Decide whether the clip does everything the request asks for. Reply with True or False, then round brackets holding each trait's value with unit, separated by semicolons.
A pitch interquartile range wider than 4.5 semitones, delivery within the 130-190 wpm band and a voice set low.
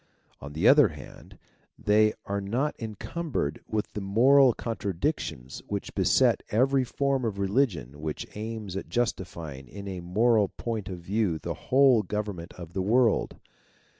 True (5.1 semitones; 150 wpm; 105 Hz)